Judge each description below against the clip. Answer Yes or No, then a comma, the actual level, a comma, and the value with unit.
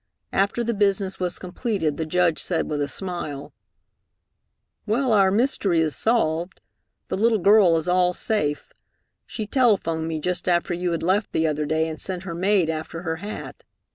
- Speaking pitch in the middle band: Yes, medium, 180 Hz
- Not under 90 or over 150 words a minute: No, average, 170 wpm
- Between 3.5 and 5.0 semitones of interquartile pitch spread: Yes, average, 4.0 semitones